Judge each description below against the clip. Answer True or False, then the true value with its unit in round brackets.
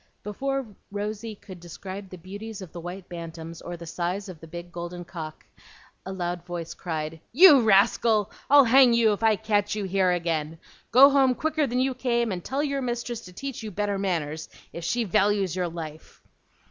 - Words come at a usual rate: True (190 wpm)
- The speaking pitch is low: False (195 Hz)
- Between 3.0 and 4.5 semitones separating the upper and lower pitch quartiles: False (5.2 semitones)